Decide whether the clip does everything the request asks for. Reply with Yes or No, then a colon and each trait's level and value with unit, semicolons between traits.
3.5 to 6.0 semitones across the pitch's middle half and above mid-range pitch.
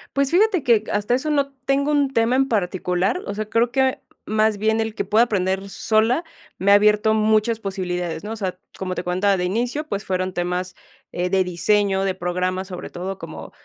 Yes: average, 4.0 semitones; high, 210 Hz